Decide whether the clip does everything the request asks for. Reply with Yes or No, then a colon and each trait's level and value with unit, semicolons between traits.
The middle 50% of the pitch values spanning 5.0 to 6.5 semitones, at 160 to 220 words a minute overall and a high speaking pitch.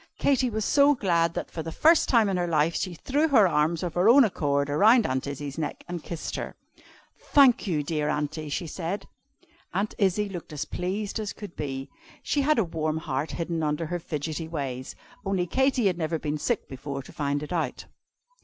No: wide, 5.6 semitones; average, 200 wpm; medium, 170 Hz